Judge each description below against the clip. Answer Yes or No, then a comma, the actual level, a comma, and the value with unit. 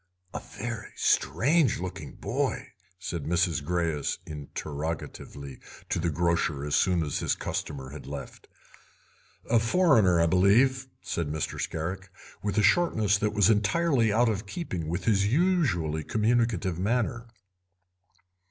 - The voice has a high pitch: No, very low, 95 Hz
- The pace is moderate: No, slow, 130 wpm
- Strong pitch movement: Yes, wide, 6.4 semitones